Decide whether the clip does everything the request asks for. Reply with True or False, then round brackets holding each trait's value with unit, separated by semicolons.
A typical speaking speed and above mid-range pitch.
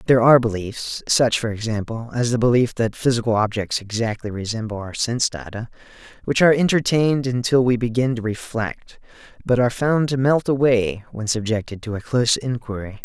False (165 wpm; 115 Hz)